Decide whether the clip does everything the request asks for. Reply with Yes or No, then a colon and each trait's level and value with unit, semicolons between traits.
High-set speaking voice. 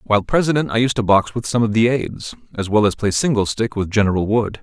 No: low, 110 Hz